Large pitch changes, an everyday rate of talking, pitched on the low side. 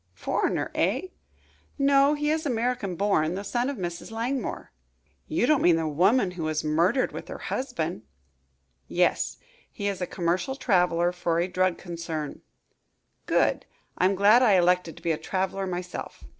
No: wide, 6.0 semitones; average, 155 wpm; medium, 185 Hz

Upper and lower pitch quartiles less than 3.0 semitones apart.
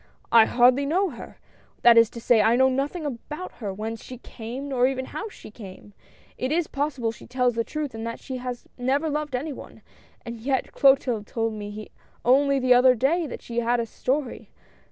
No: average, 3.3 semitones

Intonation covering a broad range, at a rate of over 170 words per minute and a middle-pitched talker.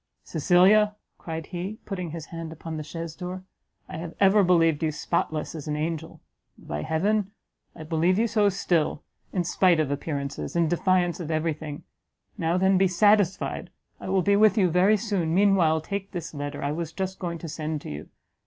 No: average, 3.2 semitones; average, 190 wpm; medium, 170 Hz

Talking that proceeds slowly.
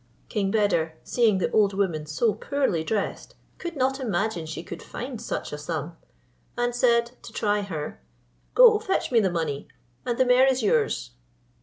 No: average, 170 wpm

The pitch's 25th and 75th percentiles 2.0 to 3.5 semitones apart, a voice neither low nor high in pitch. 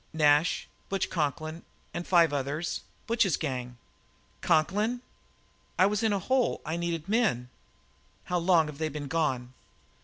No: average, 4.6 semitones; medium, 165 Hz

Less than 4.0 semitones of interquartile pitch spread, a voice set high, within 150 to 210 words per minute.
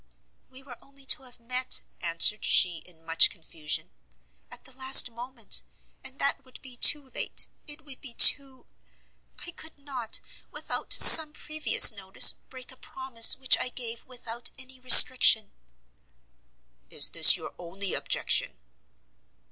No: average, 3.0 semitones; very high, 255 Hz; average, 140 wpm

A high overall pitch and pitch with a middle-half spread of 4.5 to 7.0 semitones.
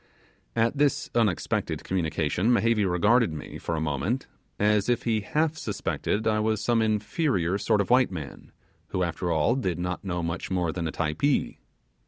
No: low, 105 Hz; average, 5.1 semitones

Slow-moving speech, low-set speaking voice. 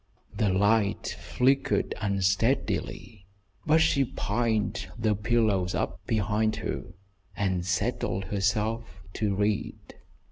Yes: slow, 100 wpm; low, 105 Hz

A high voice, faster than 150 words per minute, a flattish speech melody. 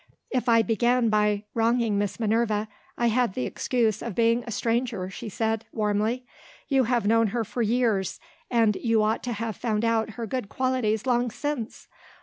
Yes: high, 230 Hz; average, 175 wpm; narrow, 2.1 semitones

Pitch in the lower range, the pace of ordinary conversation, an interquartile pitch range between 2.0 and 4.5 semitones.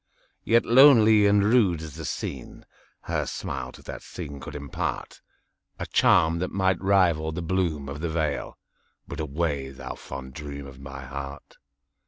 No: very low, 80 Hz; average, 145 wpm; average, 5.3 semitones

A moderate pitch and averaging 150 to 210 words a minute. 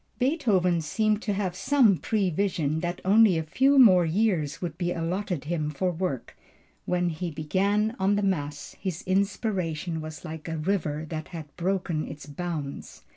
Yes: medium, 175 Hz; average, 160 wpm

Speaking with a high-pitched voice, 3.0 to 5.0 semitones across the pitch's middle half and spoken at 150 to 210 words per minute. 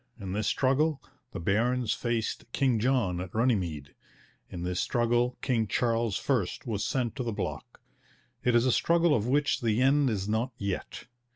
No: low, 120 Hz; average, 3.8 semitones; average, 170 wpm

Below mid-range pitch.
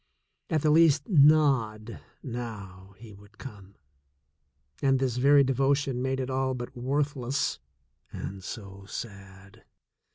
Yes: low, 125 Hz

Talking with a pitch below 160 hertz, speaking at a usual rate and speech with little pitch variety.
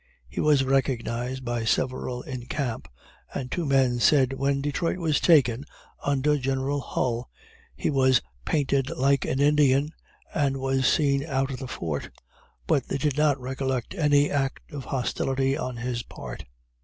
Yes: low, 135 Hz; average, 155 wpm; narrow, 2.0 semitones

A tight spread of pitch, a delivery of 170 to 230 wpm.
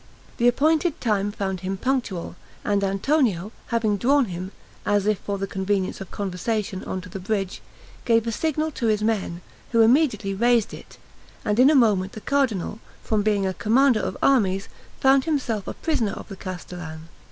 No: average, 4.2 semitones; average, 175 wpm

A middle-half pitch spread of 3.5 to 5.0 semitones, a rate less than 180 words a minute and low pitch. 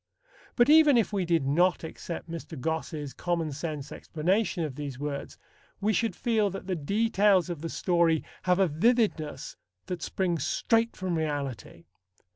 No: average, 4.6 semitones; average, 155 wpm; medium, 170 Hz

